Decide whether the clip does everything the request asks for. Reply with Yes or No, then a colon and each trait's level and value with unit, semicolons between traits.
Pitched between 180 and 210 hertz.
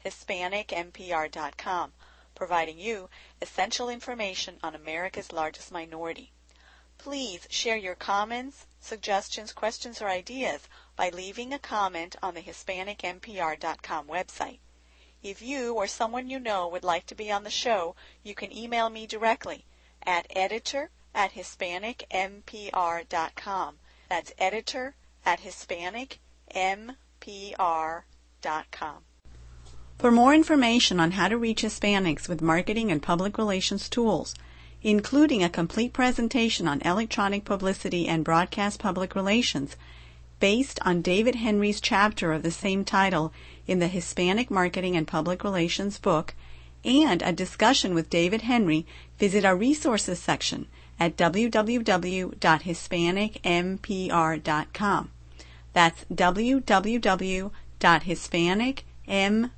Yes: high, 190 Hz